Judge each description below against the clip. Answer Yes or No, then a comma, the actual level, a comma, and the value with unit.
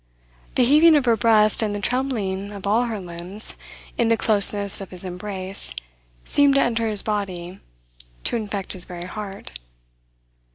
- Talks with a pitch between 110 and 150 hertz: No, high, 205 Hz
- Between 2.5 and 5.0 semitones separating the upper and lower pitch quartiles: Yes, average, 3.3 semitones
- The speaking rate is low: No, average, 160 wpm